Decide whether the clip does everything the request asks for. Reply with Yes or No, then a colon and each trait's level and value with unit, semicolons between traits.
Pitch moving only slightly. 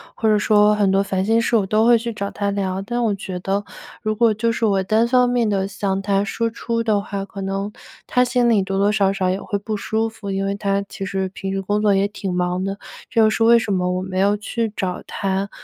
Yes: narrow, 2.2 semitones